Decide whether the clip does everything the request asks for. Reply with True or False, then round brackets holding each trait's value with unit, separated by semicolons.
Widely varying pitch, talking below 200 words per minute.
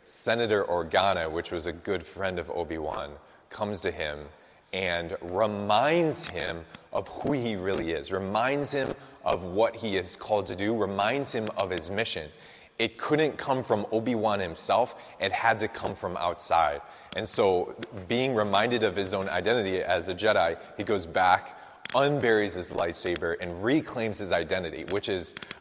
True (6.4 semitones; 165 wpm)